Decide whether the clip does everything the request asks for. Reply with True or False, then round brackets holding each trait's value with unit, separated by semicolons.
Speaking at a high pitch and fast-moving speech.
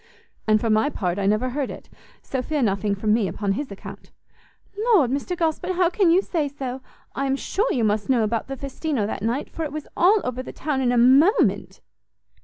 True (265 Hz; 215 wpm)